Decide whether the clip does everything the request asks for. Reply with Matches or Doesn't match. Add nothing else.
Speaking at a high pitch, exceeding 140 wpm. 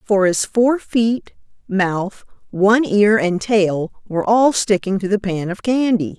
Matches